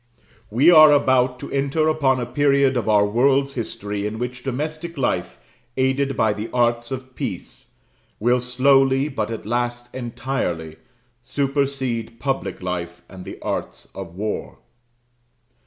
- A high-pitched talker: No, low, 125 Hz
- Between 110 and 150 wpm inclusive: Yes, average, 140 wpm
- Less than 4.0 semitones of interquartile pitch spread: Yes, average, 3.6 semitones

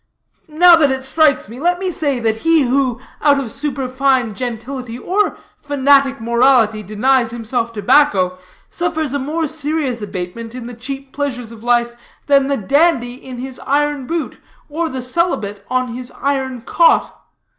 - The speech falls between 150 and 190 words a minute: Yes, average, 155 wpm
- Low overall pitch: No, very high, 265 Hz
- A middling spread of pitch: Yes, average, 3.5 semitones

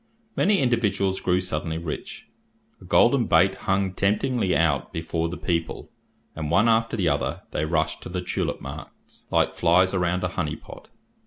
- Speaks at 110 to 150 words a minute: No, average, 165 wpm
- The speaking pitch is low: Yes, very low, 90 Hz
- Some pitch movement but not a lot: Yes, average, 3.2 semitones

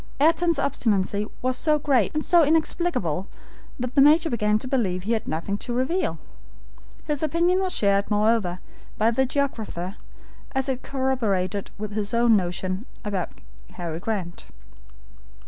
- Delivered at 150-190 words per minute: No, average, 140 wpm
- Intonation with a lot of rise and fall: Yes, wide, 5.9 semitones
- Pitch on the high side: Yes, high, 230 Hz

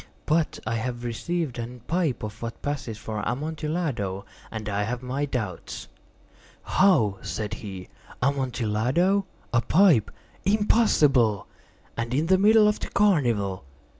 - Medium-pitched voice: No, low, 125 Hz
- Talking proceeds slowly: Yes, slow, 130 wpm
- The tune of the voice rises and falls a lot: Yes, wide, 7.0 semitones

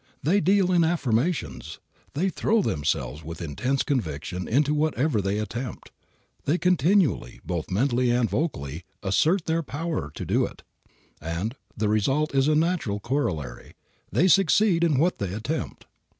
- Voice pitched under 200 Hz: Yes, low, 135 Hz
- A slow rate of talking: No, average, 145 wpm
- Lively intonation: Yes, wide, 8.6 semitones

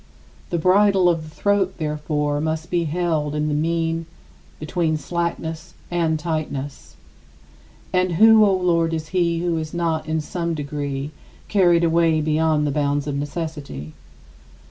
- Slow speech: No, average, 145 wpm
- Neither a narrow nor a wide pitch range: No, narrow, 2.2 semitones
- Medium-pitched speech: Yes, medium, 160 Hz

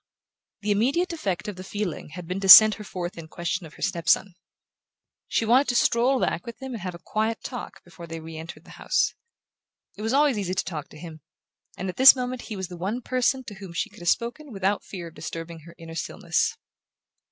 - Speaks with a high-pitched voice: Yes, high, 195 Hz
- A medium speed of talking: No, fast, 230 wpm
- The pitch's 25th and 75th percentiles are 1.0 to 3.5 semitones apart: No, wide, 5.5 semitones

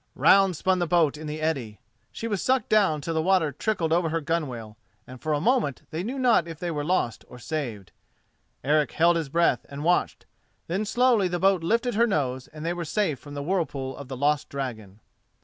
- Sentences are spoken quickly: Yes, fast, 215 wpm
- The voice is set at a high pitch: No, medium, 160 Hz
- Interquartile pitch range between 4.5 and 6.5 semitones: Yes, average, 4.8 semitones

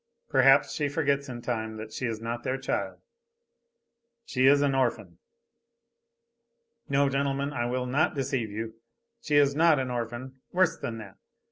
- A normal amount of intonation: Yes, average, 3.1 semitones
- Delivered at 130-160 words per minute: Yes, average, 155 wpm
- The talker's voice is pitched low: Yes, low, 130 Hz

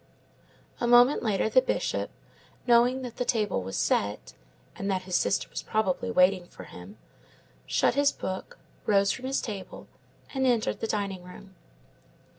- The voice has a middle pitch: No, high, 210 Hz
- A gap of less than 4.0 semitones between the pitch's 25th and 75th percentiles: No, average, 4.5 semitones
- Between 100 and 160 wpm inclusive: Yes, average, 155 wpm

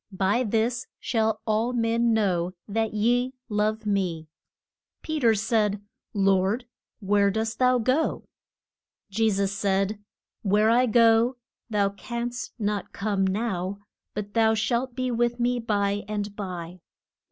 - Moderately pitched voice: No, high, 215 Hz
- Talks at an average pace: No, slow, 130 wpm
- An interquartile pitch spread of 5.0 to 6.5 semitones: No, average, 2.8 semitones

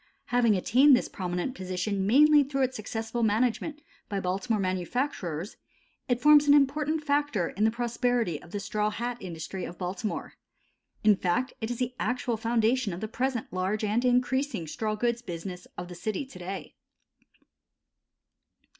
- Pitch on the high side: Yes, high, 225 Hz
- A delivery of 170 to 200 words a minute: No, average, 155 wpm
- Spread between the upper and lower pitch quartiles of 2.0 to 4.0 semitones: No, average, 5.0 semitones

